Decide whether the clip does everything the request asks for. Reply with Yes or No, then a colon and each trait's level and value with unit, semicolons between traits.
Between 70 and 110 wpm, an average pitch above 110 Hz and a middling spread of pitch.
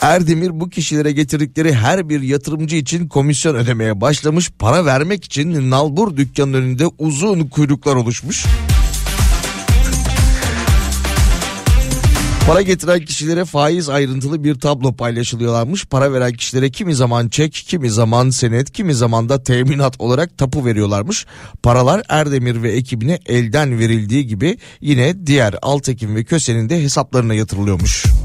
No: average, 125 wpm; medium, 140 Hz; average, 4.5 semitones